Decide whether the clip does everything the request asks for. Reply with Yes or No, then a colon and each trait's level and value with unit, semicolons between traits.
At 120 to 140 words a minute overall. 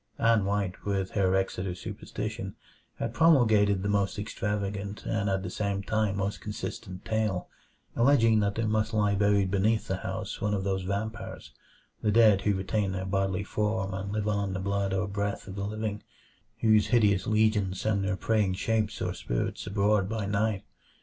No: average, 175 wpm